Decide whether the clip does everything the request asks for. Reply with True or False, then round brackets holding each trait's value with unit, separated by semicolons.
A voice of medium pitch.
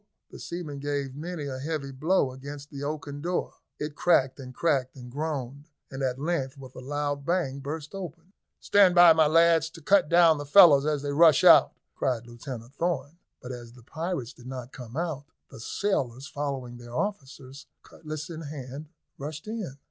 True (145 Hz)